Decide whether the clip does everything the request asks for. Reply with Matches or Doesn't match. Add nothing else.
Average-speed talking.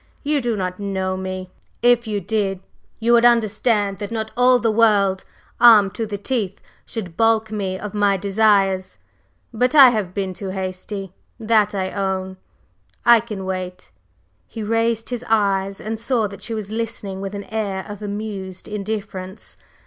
Matches